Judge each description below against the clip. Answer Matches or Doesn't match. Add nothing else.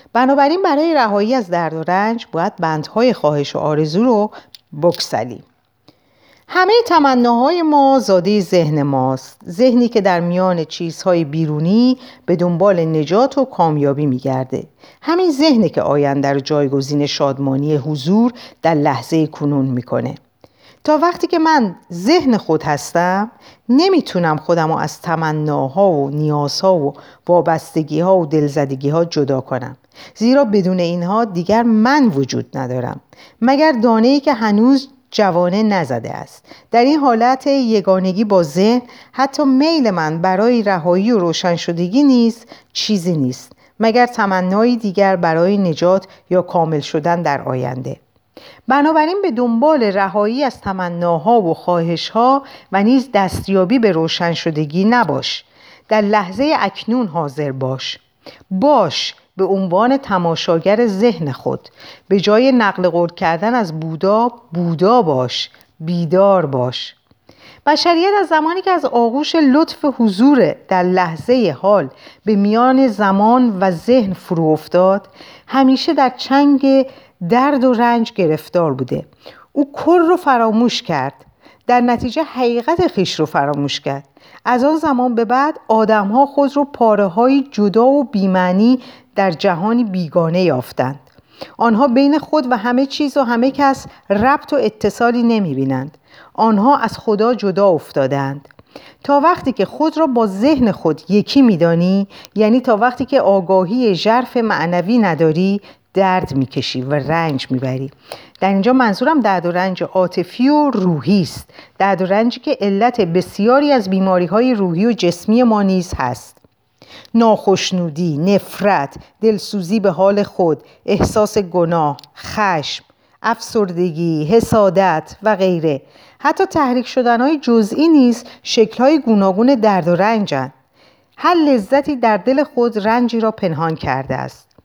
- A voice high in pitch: Matches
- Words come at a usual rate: Matches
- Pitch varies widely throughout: Matches